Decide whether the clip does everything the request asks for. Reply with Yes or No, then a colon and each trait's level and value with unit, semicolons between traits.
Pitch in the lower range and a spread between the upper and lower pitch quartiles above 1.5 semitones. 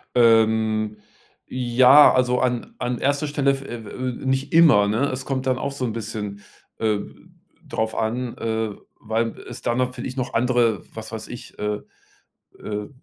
Yes: low, 120 Hz; average, 2.7 semitones